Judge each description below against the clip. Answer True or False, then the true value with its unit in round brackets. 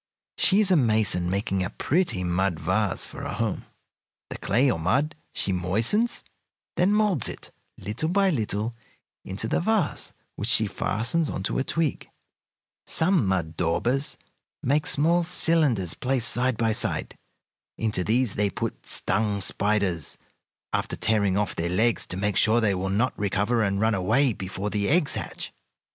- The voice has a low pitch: True (110 Hz)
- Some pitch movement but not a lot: False (6.7 semitones)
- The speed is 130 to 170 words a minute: True (160 wpm)